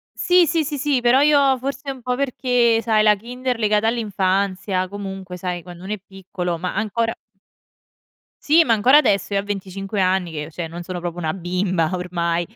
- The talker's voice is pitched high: Yes, high, 200 Hz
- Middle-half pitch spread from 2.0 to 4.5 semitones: No, wide, 5.4 semitones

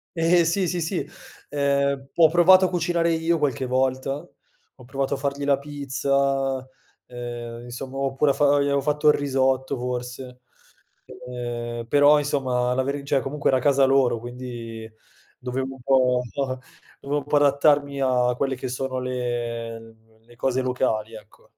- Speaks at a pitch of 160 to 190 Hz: No, low, 135 Hz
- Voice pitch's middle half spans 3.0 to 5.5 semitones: No, narrow, 2.4 semitones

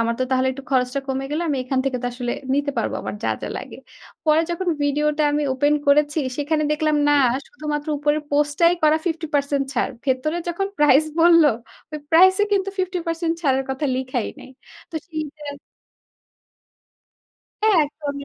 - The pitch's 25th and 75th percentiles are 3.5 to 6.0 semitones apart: No, average, 2.9 semitones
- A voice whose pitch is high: Yes, very high, 295 Hz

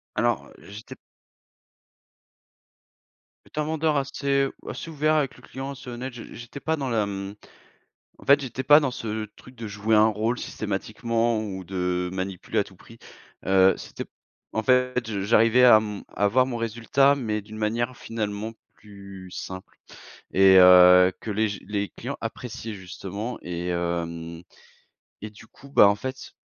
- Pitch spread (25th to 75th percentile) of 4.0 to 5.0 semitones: Yes, average, 4.5 semitones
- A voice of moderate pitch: No, low, 110 Hz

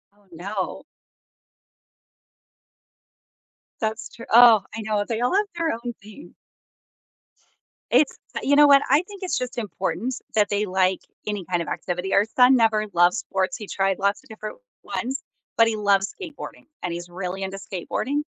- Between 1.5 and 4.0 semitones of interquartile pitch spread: No, average, 4.5 semitones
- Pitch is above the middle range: Yes, high, 215 Hz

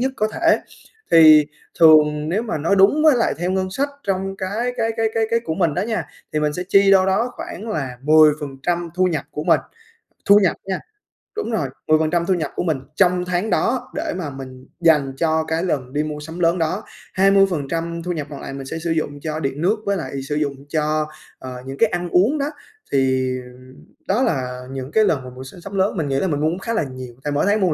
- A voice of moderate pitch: Yes, medium, 165 Hz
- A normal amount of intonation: Yes, average, 4.8 semitones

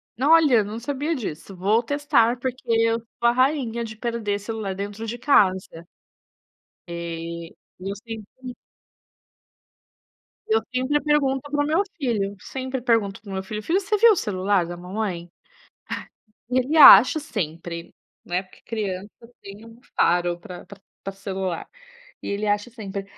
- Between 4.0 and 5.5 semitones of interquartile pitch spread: Yes, average, 5.1 semitones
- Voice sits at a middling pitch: No, high, 220 Hz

